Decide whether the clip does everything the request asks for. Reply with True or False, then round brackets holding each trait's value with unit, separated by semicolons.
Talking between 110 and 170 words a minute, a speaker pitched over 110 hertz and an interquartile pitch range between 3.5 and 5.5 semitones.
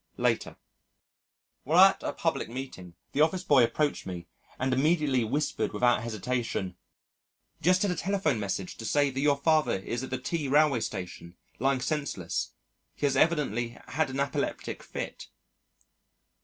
True (150 wpm; 135 Hz; 4.7 semitones)